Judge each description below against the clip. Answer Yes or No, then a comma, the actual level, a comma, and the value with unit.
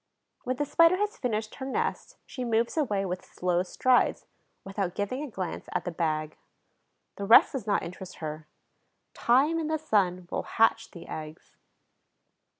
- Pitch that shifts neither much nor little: No, wide, 6.7 semitones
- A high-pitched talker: Yes, high, 210 Hz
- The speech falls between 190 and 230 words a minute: No, average, 160 wpm